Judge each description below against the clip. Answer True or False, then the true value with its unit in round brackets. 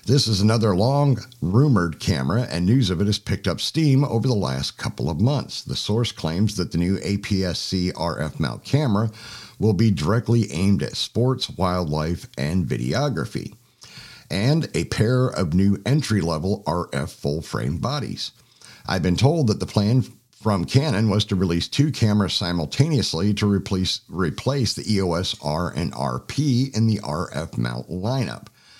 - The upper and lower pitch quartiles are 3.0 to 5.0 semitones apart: True (4.7 semitones)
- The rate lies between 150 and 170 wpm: True (165 wpm)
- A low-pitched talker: True (100 Hz)